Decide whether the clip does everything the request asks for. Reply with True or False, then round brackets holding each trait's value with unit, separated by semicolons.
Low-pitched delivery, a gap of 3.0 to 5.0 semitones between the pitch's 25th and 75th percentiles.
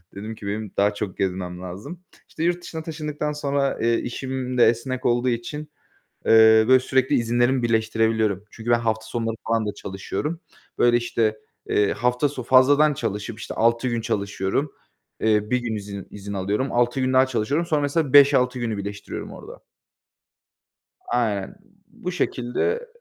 True (120 Hz; 3.6 semitones)